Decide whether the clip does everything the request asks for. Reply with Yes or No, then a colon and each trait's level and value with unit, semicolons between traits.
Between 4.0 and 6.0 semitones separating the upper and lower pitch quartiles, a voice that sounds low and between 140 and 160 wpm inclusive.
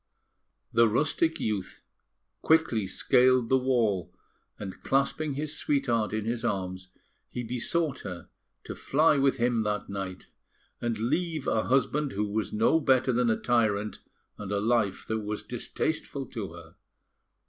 Yes: average, 4.3 semitones; low, 115 Hz; average, 145 wpm